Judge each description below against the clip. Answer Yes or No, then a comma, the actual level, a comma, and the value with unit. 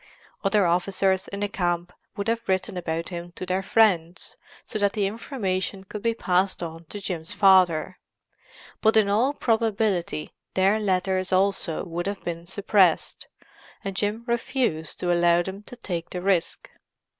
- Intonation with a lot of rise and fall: No, average, 2.8 semitones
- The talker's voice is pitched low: No, high, 190 Hz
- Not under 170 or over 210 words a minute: No, average, 155 wpm